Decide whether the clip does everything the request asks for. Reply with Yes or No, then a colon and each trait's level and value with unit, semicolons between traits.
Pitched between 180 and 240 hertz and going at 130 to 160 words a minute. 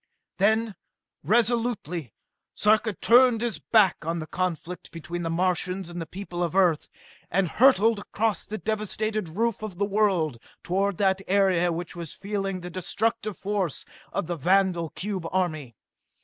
Yes: high, 190 Hz; average, 150 wpm